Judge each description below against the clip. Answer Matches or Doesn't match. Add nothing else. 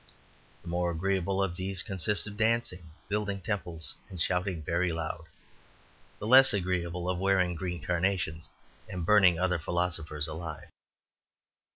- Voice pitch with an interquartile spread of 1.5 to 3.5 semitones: Matches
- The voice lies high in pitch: Doesn't match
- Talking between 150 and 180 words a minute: Doesn't match